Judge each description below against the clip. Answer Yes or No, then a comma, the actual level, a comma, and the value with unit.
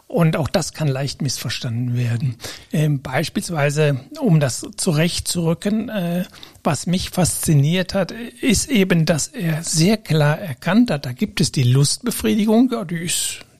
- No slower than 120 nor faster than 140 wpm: Yes, average, 135 wpm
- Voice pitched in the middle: Yes, medium, 165 Hz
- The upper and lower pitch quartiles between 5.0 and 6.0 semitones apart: Yes, average, 5.3 semitones